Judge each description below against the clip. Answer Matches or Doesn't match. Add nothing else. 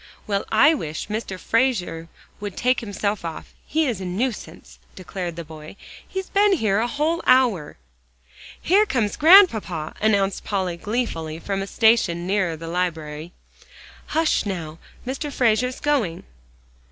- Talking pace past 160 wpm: Doesn't match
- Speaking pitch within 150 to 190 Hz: Doesn't match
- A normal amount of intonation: Doesn't match